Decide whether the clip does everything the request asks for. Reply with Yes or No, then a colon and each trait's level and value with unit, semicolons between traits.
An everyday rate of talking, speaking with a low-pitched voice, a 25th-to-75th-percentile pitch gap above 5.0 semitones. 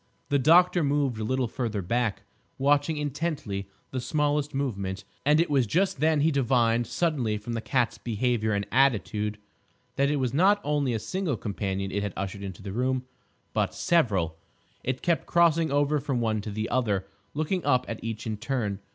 Yes: average, 180 wpm; low, 125 Hz; wide, 5.5 semitones